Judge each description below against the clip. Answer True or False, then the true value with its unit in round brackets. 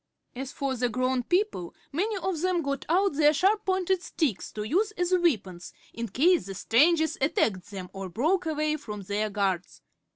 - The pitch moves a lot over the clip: True (9.0 semitones)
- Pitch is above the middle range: True (285 Hz)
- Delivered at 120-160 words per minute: False (175 wpm)